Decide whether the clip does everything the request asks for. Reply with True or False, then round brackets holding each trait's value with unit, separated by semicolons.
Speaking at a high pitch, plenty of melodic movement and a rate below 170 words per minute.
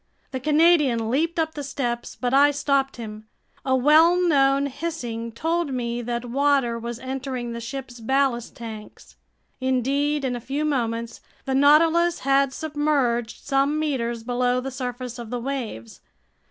False (265 Hz; 3.3 semitones; 150 wpm)